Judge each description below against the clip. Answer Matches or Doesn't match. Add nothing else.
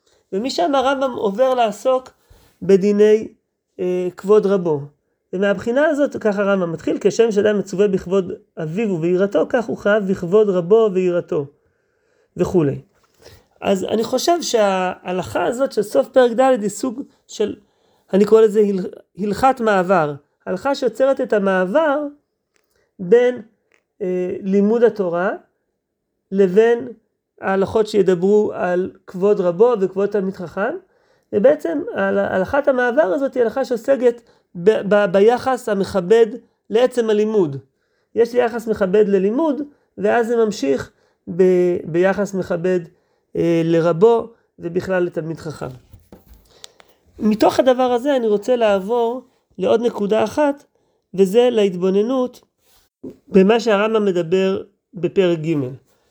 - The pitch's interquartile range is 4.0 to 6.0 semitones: Matches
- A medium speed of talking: Matches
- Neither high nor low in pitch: Doesn't match